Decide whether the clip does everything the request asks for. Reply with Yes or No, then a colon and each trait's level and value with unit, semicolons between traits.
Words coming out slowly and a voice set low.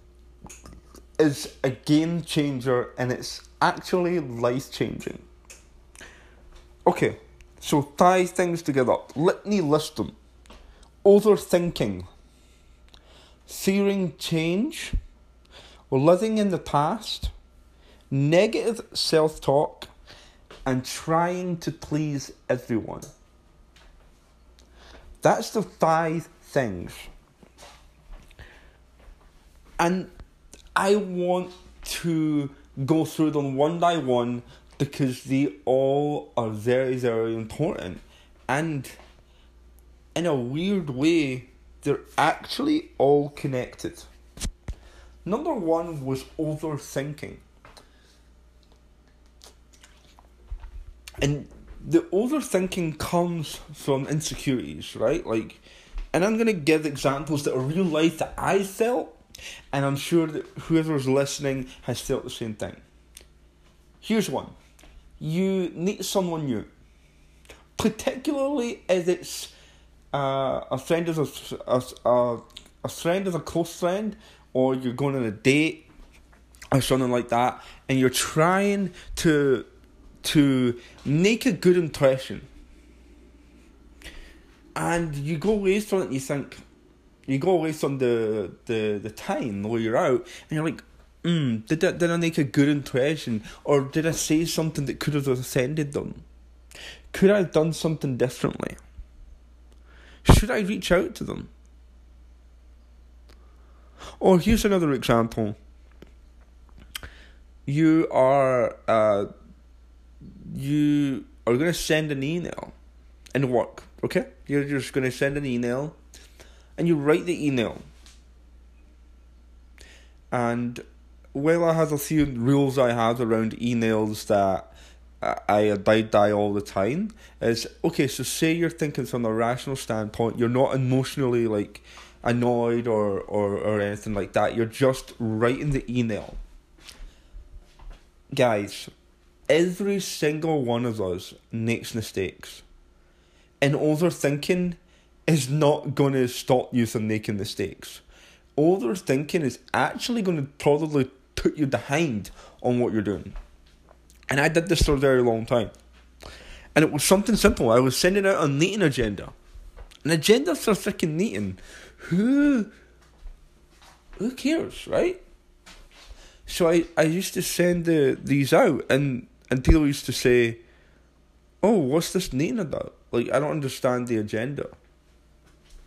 Yes: slow, 120 wpm; low, 130 Hz